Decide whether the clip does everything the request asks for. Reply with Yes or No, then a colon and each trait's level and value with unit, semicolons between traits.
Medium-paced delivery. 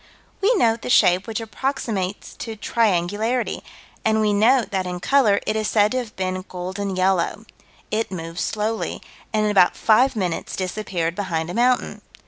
Yes: average, 165 wpm